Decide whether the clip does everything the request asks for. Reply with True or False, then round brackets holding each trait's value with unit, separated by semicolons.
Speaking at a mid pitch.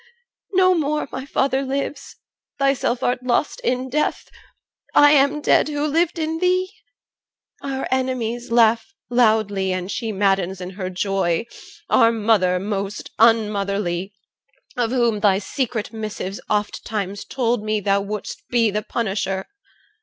False (225 Hz)